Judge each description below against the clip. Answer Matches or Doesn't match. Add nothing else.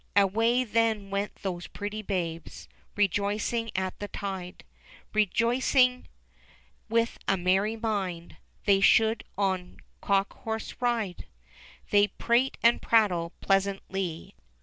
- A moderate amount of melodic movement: Matches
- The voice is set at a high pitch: Matches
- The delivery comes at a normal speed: Doesn't match